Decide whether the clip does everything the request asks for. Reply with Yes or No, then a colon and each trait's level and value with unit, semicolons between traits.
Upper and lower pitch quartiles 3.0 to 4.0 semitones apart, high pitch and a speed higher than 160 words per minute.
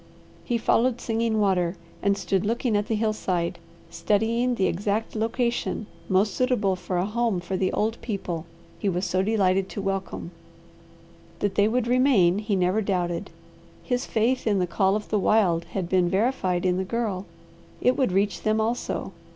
Yes: average, 3.4 semitones; high, 205 Hz; average, 170 wpm